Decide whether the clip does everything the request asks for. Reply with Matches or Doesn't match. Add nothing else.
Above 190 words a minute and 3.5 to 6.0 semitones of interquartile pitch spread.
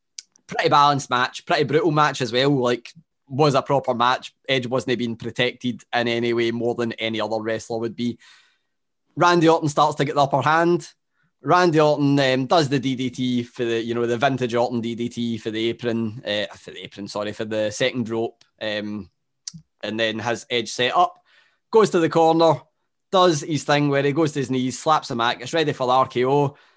Matches